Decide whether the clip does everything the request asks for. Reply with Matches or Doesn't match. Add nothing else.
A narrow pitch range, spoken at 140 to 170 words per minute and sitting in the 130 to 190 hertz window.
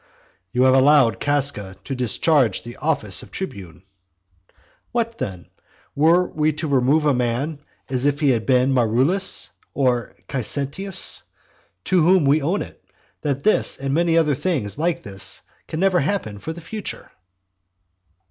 Doesn't match